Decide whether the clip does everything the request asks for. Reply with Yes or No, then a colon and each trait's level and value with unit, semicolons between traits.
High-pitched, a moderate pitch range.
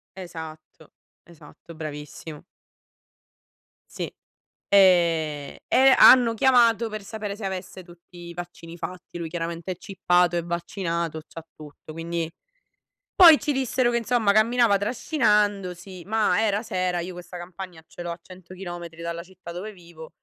No: medium, 180 Hz; average, 3.7 semitones